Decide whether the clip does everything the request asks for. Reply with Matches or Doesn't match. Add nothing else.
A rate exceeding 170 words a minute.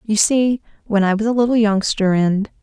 Matches